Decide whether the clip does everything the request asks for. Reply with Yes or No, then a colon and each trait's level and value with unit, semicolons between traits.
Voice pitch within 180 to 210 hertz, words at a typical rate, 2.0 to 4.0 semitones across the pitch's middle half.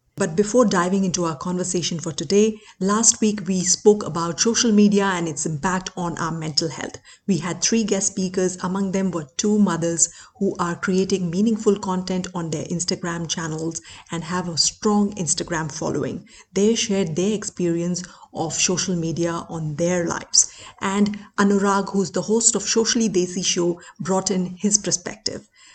Yes: medium, 185 Hz; average, 165 wpm; average, 3.0 semitones